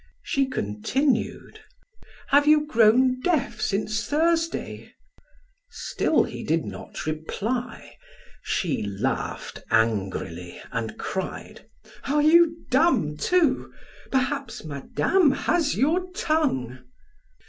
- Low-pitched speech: No, very high, 255 Hz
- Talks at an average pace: No, slow, 95 wpm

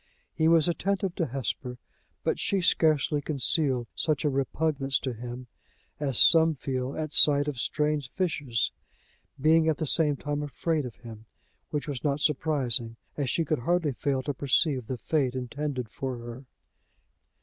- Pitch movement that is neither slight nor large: Yes, average, 3.4 semitones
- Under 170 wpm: Yes, average, 160 wpm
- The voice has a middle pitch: Yes, medium, 145 Hz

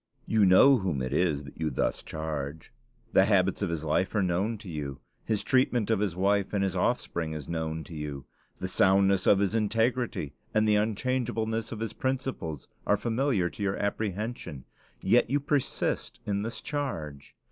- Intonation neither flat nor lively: No, wide, 5.7 semitones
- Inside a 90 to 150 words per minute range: No, average, 180 wpm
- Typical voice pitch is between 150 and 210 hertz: No, low, 100 Hz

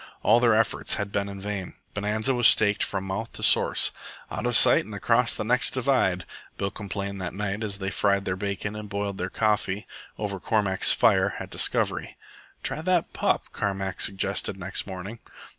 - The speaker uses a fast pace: No, average, 175 wpm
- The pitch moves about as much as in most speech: No, narrow, 1.9 semitones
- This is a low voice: Yes, low, 100 Hz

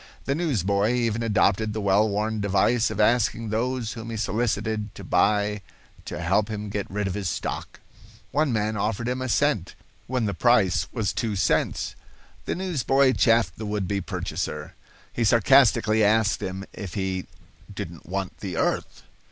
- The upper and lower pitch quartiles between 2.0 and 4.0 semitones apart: Yes, narrow, 2.6 semitones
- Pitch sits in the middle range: No, low, 110 Hz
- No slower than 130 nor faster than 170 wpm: Yes, average, 165 wpm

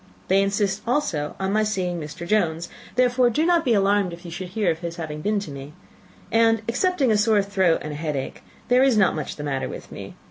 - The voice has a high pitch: Yes, high, 195 Hz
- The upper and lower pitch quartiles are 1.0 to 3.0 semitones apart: No, average, 5.3 semitones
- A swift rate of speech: Yes, fast, 225 wpm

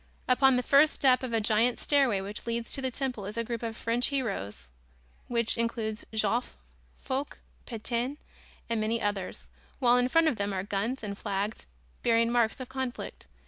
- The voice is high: Yes, high, 235 Hz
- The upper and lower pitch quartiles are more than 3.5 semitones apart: No, average, 2.9 semitones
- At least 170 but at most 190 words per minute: Yes, average, 180 wpm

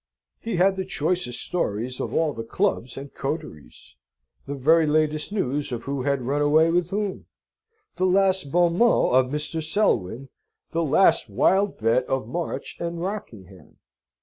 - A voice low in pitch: No, medium, 150 Hz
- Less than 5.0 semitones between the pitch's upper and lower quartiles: No, wide, 5.6 semitones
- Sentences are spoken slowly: No, average, 155 wpm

